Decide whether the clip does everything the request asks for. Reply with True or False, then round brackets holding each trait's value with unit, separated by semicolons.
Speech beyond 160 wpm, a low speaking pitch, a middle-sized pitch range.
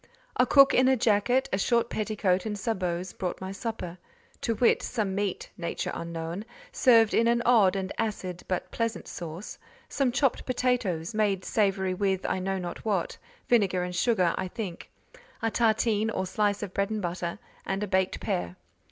False (170 wpm; 200 Hz; 3.7 semitones)